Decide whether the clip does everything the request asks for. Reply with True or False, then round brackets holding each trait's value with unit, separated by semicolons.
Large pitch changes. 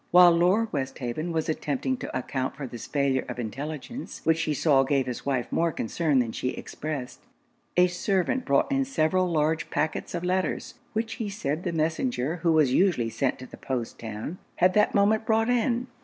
True (5.8 semitones)